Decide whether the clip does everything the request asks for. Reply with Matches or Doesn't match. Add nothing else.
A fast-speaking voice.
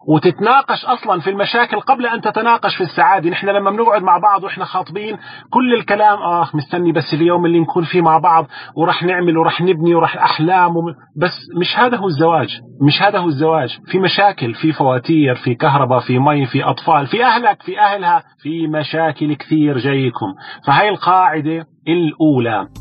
Matches